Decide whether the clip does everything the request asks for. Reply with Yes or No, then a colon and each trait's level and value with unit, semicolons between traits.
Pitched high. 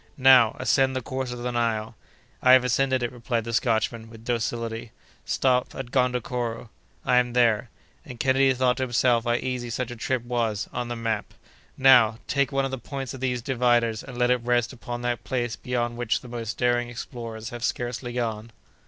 No: low, 120 Hz